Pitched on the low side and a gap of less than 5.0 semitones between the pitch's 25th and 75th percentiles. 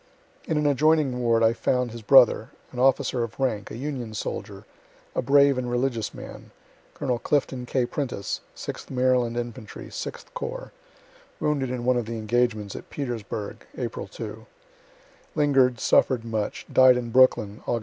Yes: low, 125 Hz; narrow, 2.4 semitones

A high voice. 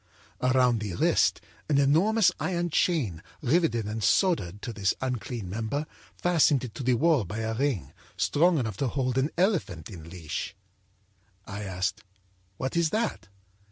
No: low, 125 Hz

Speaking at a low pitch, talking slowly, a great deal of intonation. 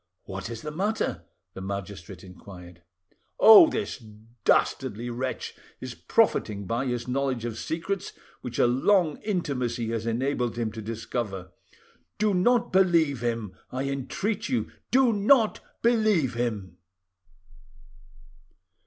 Yes: low, 125 Hz; slow, 120 wpm; wide, 8.9 semitones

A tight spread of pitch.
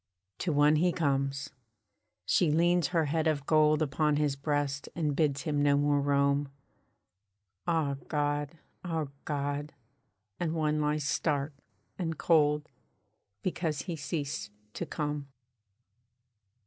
Yes: narrow, 1.9 semitones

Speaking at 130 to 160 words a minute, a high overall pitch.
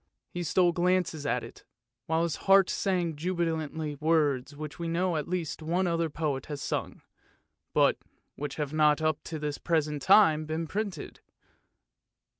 No: average, 155 wpm; medium, 160 Hz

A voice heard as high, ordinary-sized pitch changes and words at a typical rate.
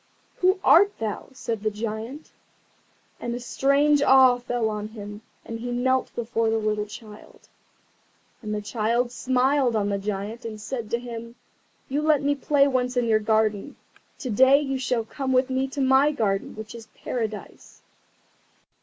Yes: high, 240 Hz; average, 3.5 semitones; average, 165 wpm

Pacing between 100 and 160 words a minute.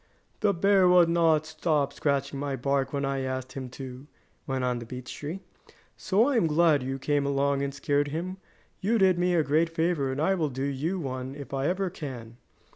No: fast, 205 wpm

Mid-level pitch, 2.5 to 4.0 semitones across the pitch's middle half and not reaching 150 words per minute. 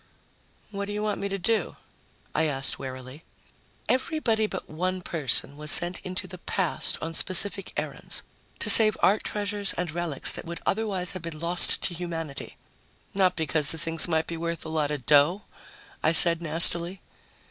No: medium, 170 Hz; average, 3.6 semitones; average, 170 wpm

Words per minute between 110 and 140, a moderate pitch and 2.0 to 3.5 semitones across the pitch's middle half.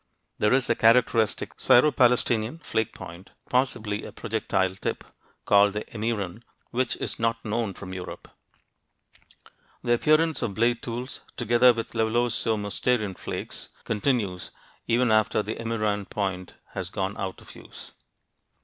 No: slow, 135 wpm; low, 110 Hz; average, 2.7 semitones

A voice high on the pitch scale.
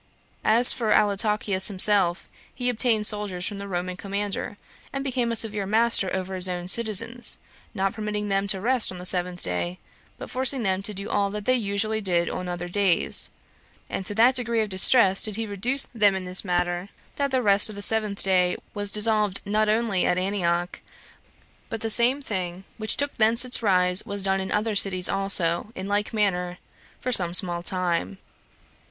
Yes: high, 200 Hz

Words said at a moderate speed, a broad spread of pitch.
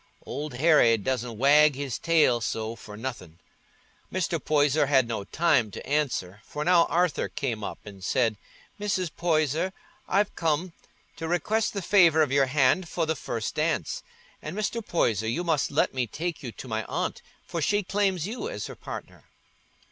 Yes: average, 170 wpm; wide, 6.0 semitones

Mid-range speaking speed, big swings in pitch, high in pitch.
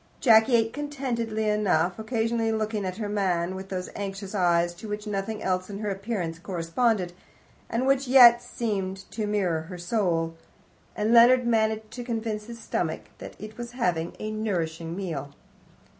No: average, 160 wpm; average, 3.9 semitones; high, 210 Hz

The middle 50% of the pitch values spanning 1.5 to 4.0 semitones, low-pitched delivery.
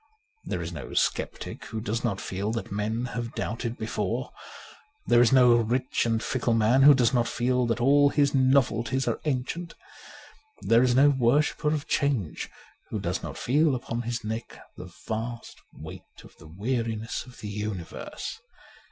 Yes: average, 2.8 semitones; low, 120 Hz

